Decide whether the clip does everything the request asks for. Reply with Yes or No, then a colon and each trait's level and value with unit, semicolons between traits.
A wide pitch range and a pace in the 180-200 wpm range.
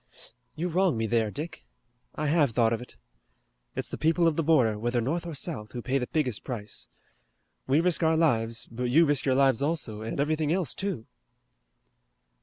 Yes: wide, 5.7 semitones; average, 190 wpm